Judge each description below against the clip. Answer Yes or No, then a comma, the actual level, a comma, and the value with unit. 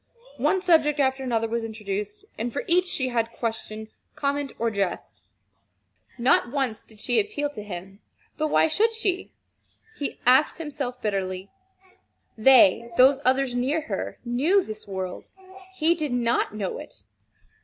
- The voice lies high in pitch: Yes, high, 245 Hz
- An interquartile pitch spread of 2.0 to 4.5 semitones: No, average, 5.2 semitones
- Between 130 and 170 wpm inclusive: Yes, average, 145 wpm